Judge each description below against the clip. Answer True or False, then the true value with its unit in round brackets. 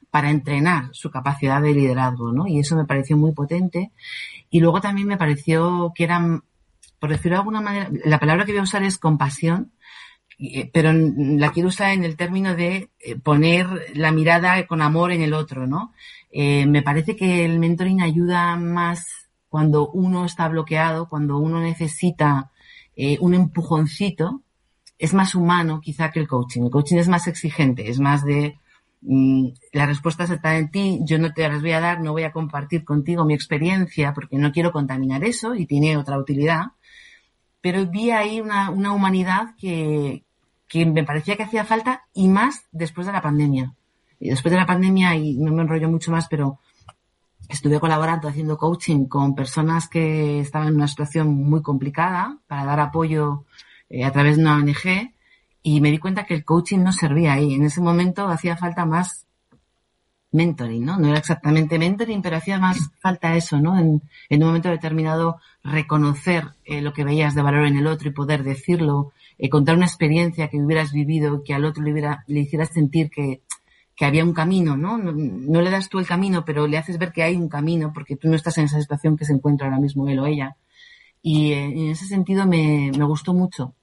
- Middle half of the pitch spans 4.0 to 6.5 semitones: False (3.1 semitones)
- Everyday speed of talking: False (195 wpm)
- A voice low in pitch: False (160 Hz)